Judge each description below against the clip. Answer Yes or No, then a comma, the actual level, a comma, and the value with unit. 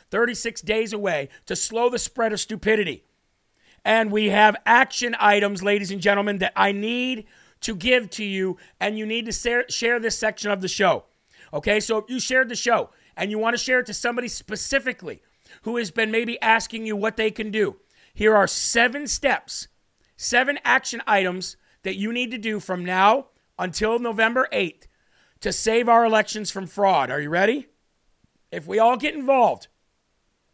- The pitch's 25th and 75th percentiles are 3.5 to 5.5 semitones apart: No, narrow, 2.5 semitones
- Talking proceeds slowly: No, average, 180 wpm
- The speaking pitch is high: Yes, high, 220 Hz